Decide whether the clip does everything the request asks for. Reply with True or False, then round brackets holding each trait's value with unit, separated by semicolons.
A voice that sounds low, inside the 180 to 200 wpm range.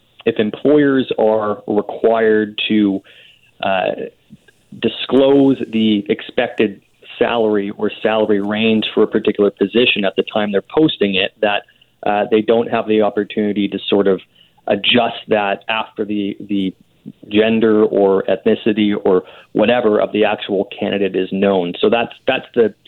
False (105 Hz; 140 wpm)